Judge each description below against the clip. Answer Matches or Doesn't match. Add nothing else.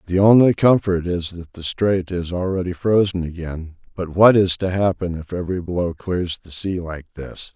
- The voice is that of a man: Matches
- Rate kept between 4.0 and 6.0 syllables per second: Matches